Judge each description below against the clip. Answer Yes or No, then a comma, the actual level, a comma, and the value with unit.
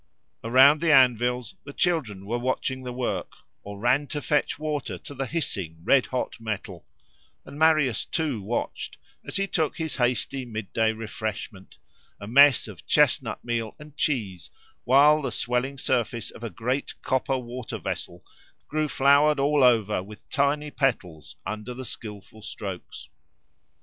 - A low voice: Yes, low, 125 Hz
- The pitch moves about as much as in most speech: Yes, average, 4.6 semitones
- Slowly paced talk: No, average, 150 wpm